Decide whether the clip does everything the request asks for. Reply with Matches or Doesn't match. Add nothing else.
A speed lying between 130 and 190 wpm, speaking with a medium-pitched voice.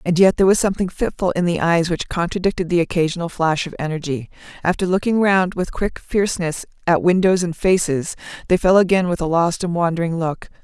Doesn't match